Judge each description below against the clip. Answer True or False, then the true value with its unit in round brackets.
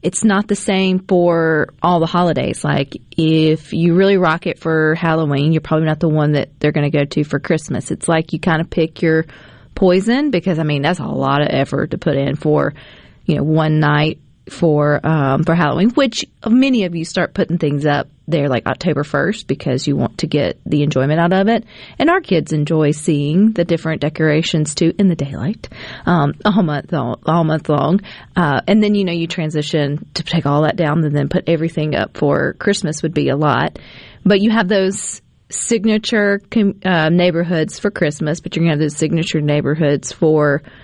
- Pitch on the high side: False (160 Hz)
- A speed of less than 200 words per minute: False (205 wpm)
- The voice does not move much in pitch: False (3.3 semitones)